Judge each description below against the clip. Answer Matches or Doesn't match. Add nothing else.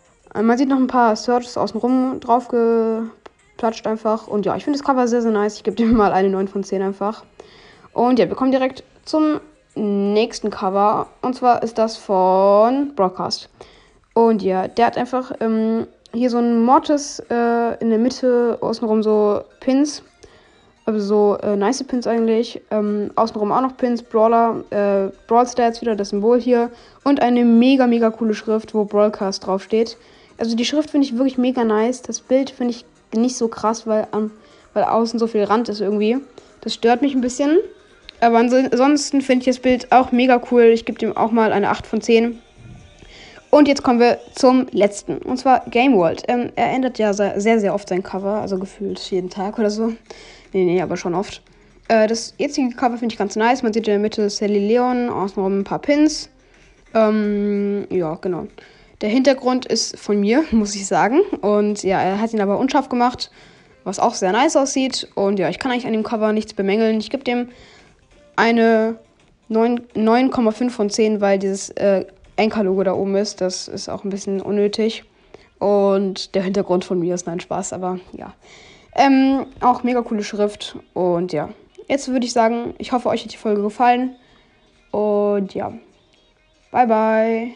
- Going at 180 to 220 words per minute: Matches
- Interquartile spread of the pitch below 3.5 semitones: Matches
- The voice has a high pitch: Matches